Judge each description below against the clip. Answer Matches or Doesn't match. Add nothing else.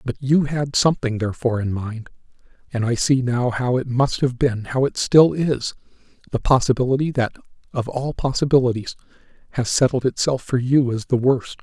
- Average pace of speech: Matches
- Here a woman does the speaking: Doesn't match